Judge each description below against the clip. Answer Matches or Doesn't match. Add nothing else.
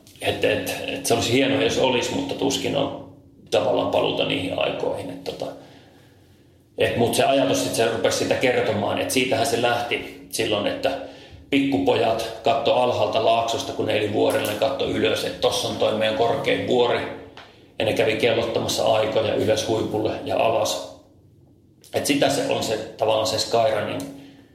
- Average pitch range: Matches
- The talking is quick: Matches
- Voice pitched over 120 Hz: Doesn't match